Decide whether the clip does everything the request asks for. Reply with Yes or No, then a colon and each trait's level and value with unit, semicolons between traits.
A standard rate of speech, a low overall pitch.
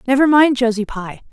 No: average, 180 wpm; very high, 250 Hz